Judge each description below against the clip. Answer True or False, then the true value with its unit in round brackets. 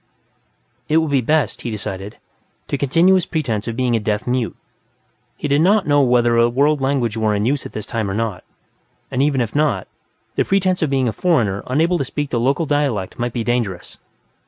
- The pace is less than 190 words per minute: False (205 wpm)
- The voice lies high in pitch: False (130 Hz)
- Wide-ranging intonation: False (4.6 semitones)